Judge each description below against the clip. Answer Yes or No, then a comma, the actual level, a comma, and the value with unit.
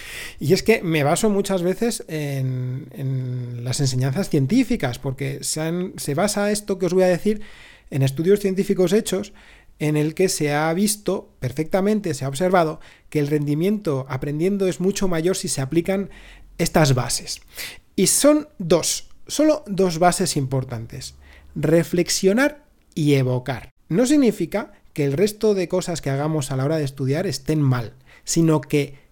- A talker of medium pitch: Yes, medium, 170 Hz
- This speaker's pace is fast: No, average, 160 wpm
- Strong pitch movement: Yes, wide, 5.7 semitones